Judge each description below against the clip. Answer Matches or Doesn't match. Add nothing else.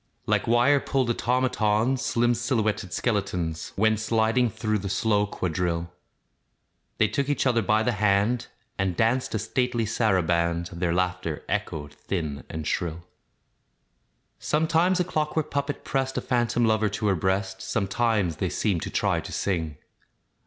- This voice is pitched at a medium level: Doesn't match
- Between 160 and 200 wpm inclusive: Doesn't match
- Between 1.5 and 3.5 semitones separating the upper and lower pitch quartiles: Doesn't match